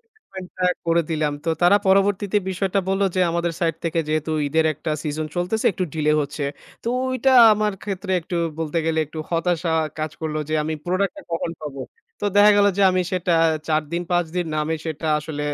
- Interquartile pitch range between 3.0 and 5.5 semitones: Yes, average, 3.4 semitones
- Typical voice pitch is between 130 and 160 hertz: No, medium, 170 Hz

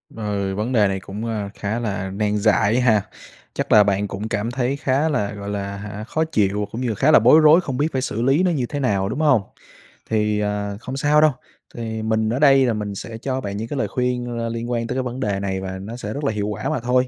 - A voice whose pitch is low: Yes, low, 110 Hz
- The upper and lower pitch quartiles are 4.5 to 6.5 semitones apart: No, average, 3.9 semitones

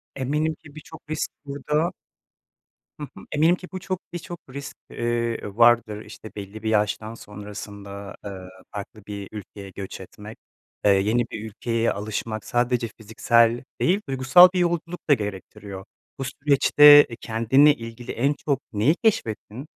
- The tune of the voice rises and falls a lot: Yes, wide, 5.7 semitones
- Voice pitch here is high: No, low, 115 Hz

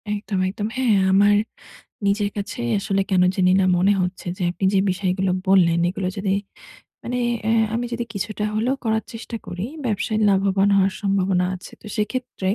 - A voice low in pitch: No, high, 195 Hz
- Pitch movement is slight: Yes, narrow, 2.2 semitones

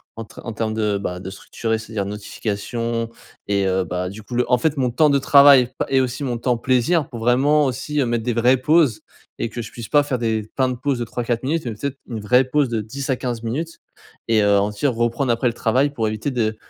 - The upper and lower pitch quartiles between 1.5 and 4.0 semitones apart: Yes, average, 3.2 semitones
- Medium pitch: No, low, 120 Hz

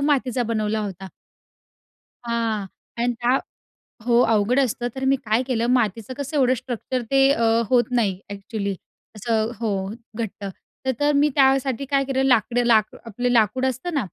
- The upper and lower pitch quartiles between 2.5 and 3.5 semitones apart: Yes, average, 3.2 semitones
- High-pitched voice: Yes, high, 240 Hz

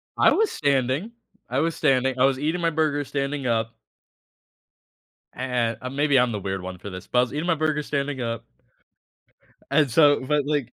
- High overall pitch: No, low, 135 Hz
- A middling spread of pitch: Yes, average, 3.3 semitones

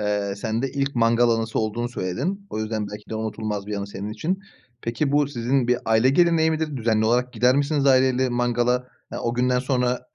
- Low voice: Yes, low, 120 Hz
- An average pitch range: Yes, average, 3.4 semitones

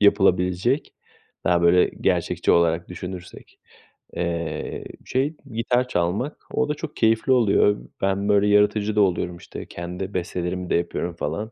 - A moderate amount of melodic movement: Yes, average, 3.9 semitones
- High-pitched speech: No, very low, 95 Hz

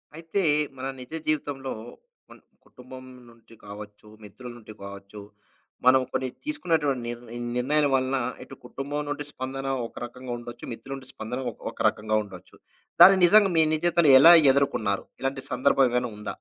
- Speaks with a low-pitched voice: Yes, low, 130 Hz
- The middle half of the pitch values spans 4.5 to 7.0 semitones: No, average, 3.8 semitones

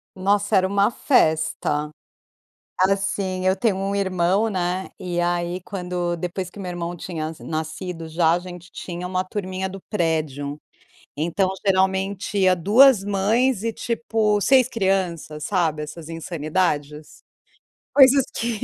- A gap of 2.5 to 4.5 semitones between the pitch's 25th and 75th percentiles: Yes, average, 2.8 semitones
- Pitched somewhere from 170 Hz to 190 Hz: Yes, medium, 185 Hz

